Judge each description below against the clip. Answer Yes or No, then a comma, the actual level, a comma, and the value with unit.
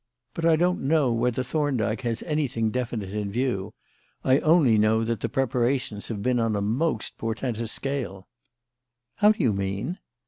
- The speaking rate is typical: Yes, average, 165 wpm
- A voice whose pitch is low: Yes, low, 120 Hz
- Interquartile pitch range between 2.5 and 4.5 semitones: Yes, average, 4.2 semitones